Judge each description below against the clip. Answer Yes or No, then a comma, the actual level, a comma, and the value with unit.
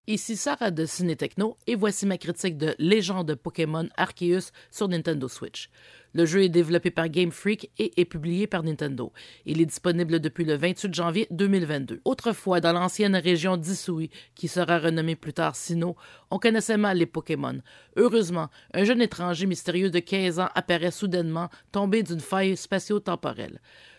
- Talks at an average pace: Yes, average, 165 wpm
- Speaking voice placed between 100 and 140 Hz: No, medium, 175 Hz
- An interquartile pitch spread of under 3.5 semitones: Yes, average, 2.8 semitones